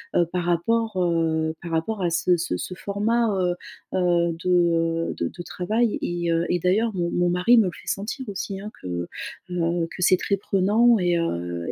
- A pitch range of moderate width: Yes, average, 3.0 semitones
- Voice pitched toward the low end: No, medium, 180 Hz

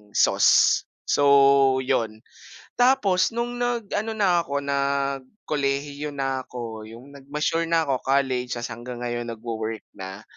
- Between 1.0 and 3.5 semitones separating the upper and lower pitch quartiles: No, average, 4.0 semitones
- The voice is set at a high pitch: No, medium, 140 Hz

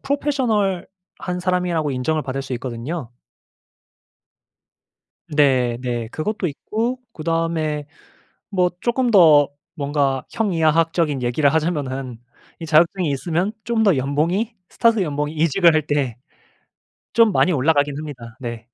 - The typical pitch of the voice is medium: Yes, medium, 155 Hz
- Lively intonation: No, average, 4.9 semitones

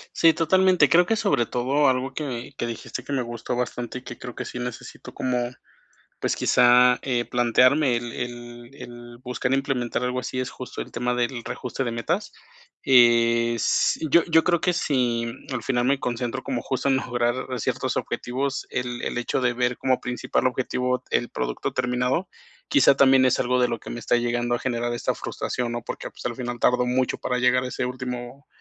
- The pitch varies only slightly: Yes, narrow, 1.6 semitones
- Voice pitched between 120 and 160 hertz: Yes, low, 125 Hz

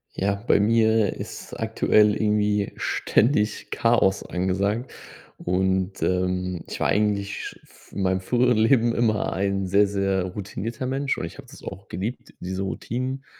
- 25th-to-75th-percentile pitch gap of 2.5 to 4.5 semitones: Yes, average, 3.1 semitones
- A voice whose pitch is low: Yes, low, 100 Hz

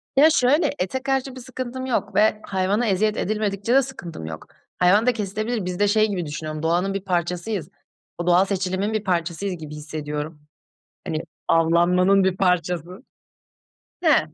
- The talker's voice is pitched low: No, high, 190 Hz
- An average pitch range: Yes, average, 4.0 semitones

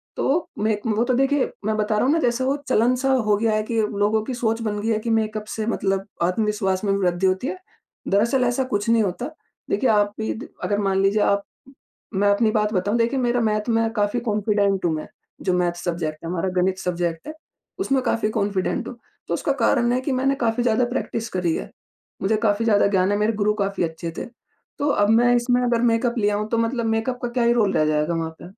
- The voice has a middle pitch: No, high, 215 Hz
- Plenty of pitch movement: No, average, 3.4 semitones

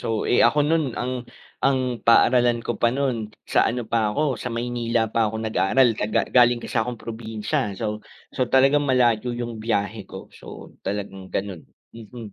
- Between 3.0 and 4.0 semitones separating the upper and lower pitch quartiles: No, narrow, 2.4 semitones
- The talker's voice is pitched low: Yes, low, 115 Hz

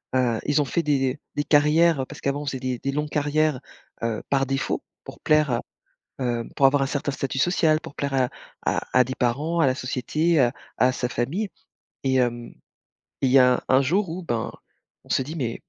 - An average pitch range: Yes, average, 3.0 semitones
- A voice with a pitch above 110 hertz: Yes, medium, 140 Hz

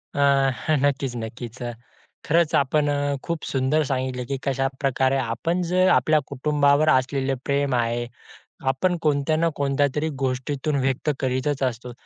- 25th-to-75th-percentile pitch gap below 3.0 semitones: Yes, narrow, 2.4 semitones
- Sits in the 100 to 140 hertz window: Yes, low, 135 Hz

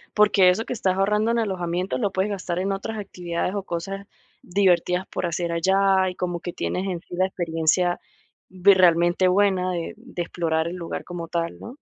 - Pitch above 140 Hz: Yes, medium, 185 Hz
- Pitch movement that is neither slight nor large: No, narrow, 2.2 semitones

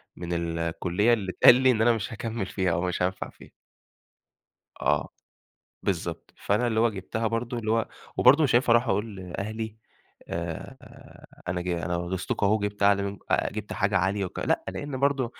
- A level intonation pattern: No, average, 4.3 semitones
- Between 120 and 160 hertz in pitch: No, low, 100 Hz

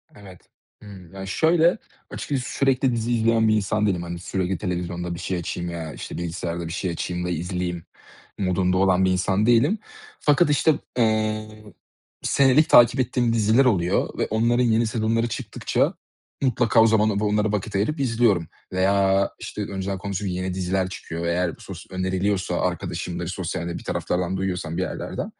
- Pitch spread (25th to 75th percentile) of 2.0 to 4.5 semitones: Yes, average, 4.0 semitones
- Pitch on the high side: No, very low, 95 Hz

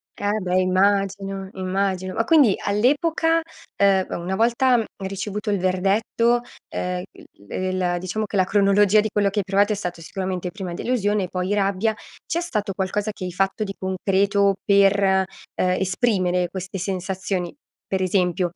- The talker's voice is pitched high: Yes, high, 195 Hz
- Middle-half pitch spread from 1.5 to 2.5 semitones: Yes, narrow, 2.0 semitones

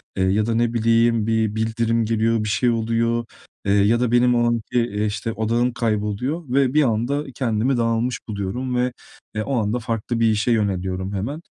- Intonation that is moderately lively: No, narrow, 2.1 semitones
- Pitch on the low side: Yes, low, 115 Hz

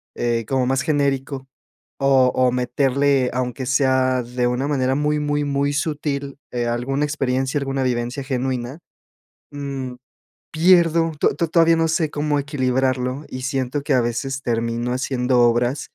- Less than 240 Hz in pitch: Yes, low, 135 Hz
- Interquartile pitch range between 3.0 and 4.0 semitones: No, narrow, 2.4 semitones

